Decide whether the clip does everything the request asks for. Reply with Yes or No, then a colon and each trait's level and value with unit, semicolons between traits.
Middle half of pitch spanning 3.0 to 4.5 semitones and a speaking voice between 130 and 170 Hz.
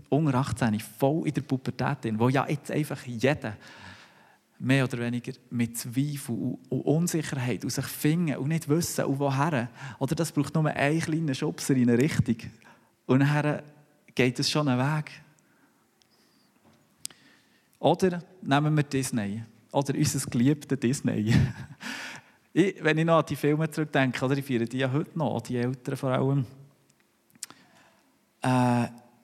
Yes: average, 3.3 semitones; low, 135 Hz